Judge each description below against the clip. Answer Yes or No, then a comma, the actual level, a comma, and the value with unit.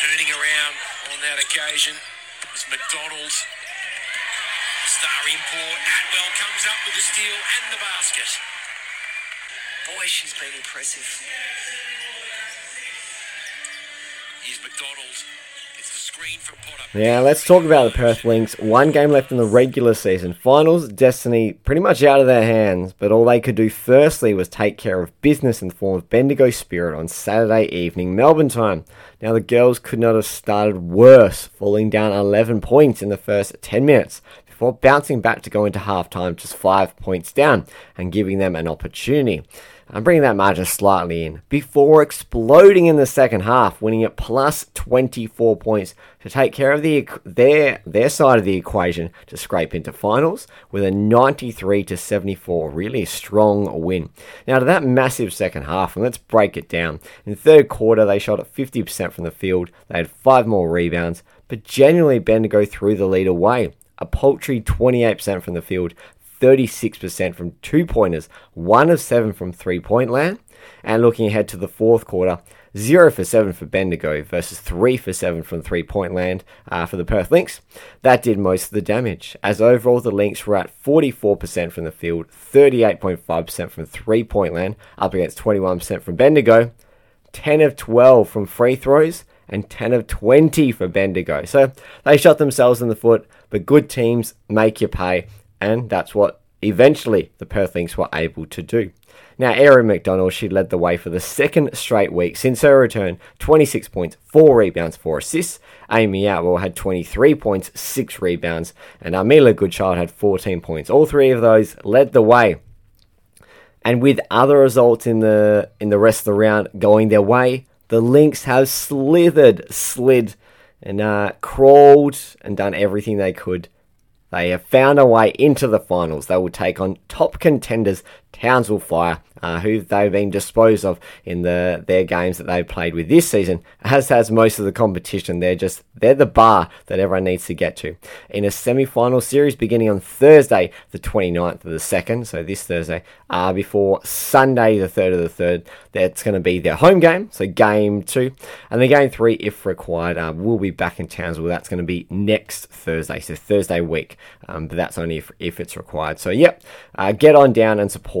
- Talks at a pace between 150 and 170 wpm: No, average, 180 wpm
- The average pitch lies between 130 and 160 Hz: No, low, 105 Hz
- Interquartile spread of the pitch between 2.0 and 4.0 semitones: No, average, 5.2 semitones